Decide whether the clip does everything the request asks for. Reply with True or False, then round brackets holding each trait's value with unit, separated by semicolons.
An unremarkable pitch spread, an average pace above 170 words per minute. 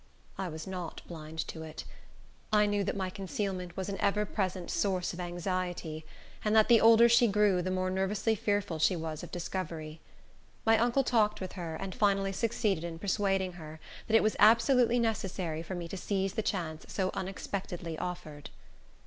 True (3.3 semitones; 180 wpm)